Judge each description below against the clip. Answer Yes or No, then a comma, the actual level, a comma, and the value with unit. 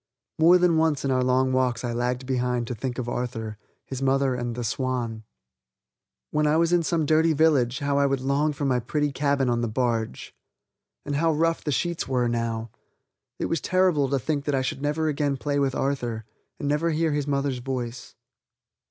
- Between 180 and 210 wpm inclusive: Yes, average, 200 wpm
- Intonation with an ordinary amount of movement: Yes, average, 3.3 semitones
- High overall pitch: No, low, 135 Hz